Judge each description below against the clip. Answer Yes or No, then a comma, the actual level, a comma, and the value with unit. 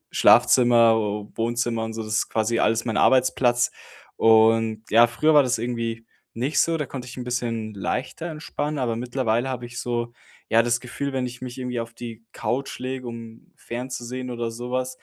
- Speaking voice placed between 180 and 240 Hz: No, low, 120 Hz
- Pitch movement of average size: No, narrow, 1.9 semitones